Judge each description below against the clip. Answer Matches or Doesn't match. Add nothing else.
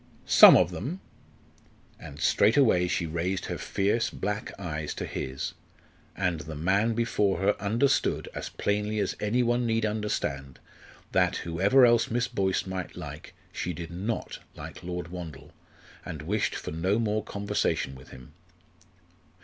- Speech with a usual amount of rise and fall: Matches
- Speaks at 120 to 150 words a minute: Matches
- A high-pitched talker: Doesn't match